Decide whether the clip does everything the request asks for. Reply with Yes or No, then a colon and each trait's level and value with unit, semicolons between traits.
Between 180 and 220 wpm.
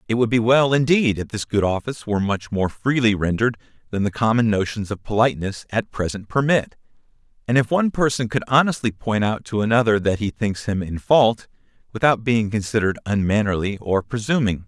Yes: average, 185 wpm